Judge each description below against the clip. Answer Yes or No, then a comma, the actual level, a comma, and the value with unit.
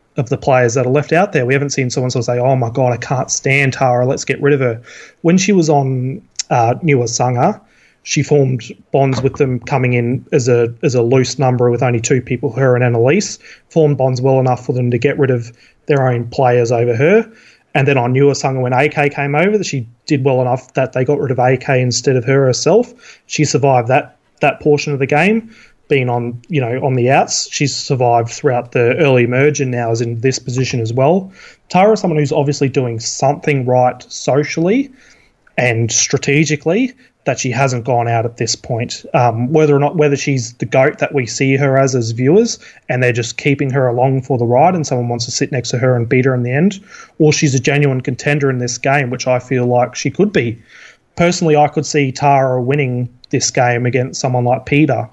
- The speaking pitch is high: No, low, 135 Hz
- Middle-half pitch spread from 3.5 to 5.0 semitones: No, average, 2.8 semitones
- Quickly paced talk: Yes, fast, 225 wpm